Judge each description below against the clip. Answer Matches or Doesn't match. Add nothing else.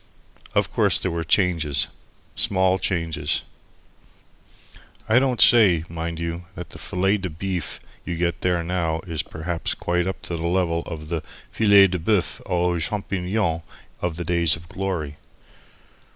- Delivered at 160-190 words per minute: Doesn't match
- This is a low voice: Matches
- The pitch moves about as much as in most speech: Doesn't match